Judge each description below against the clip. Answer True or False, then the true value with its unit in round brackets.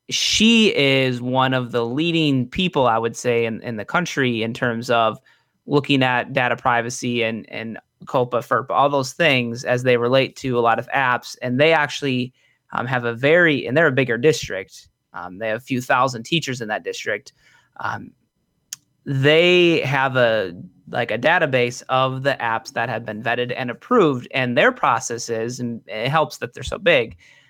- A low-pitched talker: True (125 Hz)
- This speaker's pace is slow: False (185 wpm)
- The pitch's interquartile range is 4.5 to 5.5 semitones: False (3.0 semitones)